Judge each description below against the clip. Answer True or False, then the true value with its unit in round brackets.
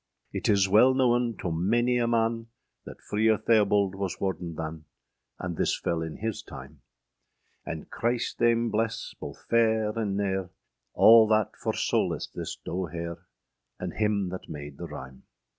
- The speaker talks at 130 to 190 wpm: True (160 wpm)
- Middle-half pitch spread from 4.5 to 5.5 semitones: True (5.0 semitones)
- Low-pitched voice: True (105 Hz)